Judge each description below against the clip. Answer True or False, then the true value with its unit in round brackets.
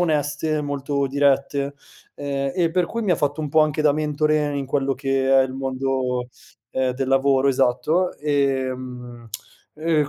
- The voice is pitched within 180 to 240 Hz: False (140 Hz)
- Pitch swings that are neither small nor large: False (2.2 semitones)